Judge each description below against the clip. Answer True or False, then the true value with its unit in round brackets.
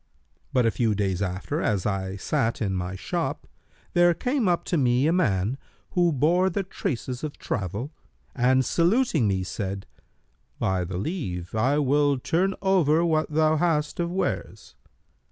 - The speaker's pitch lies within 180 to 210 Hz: False (140 Hz)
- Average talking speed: True (155 wpm)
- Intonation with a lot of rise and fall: True (9.0 semitones)